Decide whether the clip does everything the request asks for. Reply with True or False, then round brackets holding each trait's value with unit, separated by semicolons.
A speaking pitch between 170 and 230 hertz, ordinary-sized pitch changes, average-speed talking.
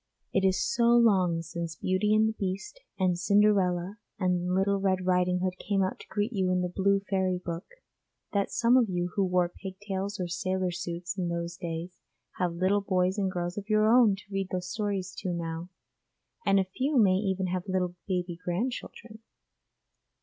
False (185 Hz; 2.1 semitones; 185 wpm)